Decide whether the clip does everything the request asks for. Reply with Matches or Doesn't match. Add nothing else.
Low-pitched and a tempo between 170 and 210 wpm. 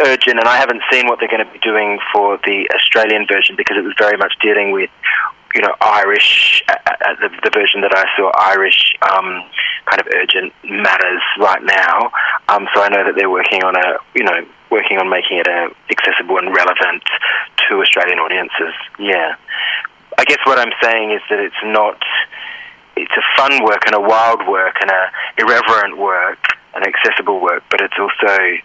Matches